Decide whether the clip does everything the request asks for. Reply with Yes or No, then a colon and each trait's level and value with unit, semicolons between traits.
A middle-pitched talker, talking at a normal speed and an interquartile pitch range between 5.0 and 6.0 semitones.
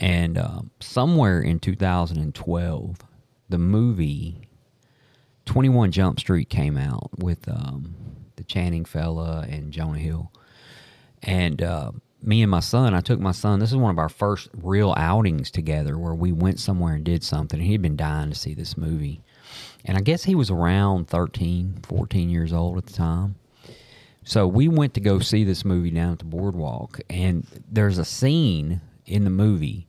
No: very low, 95 Hz; average, 175 wpm; average, 5.3 semitones